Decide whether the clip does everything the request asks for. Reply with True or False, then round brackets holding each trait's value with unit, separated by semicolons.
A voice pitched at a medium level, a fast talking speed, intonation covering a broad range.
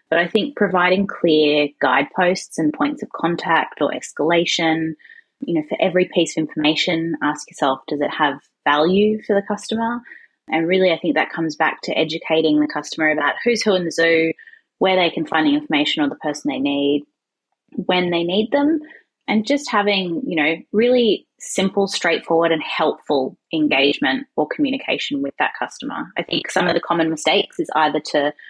False (175 Hz; 180 wpm; 6.1 semitones)